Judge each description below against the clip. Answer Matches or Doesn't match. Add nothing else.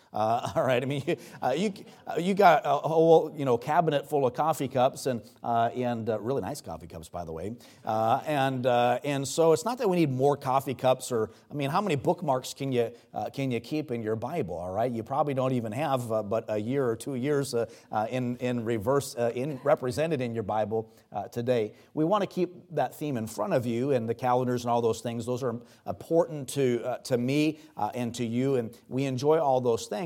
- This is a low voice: Matches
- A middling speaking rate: Doesn't match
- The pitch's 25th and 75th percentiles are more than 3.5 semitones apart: Matches